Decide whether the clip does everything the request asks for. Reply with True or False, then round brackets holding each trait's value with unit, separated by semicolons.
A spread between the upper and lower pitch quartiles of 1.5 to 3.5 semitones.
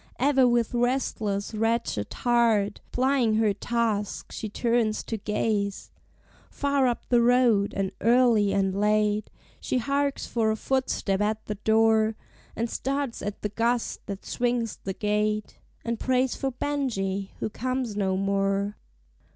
True (2.9 semitones)